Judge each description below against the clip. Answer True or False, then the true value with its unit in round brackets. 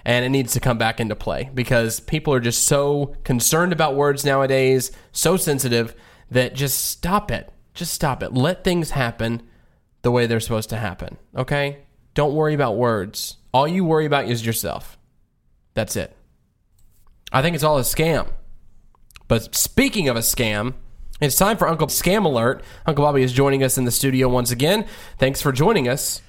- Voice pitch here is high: False (130 Hz)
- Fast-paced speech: False (180 wpm)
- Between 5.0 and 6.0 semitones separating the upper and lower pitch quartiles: False (4.1 semitones)